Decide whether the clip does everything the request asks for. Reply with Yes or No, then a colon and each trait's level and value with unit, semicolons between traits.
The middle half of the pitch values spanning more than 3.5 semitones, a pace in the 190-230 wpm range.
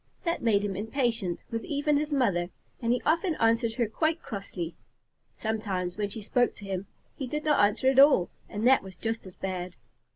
Yes: wide, 5.4 semitones; average, 195 wpm